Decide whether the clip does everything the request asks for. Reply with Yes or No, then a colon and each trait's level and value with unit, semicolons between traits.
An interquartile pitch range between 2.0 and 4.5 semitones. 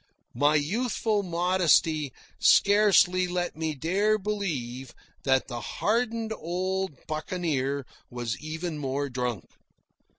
No: wide, 5.5 semitones